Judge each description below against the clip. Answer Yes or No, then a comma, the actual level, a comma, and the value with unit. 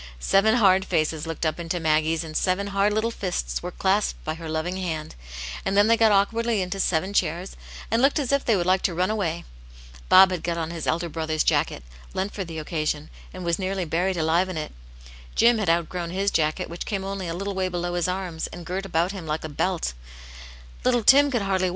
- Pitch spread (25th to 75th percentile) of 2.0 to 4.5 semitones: Yes, average, 3.4 semitones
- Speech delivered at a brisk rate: Yes, fast, 225 wpm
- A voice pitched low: No, medium, 180 Hz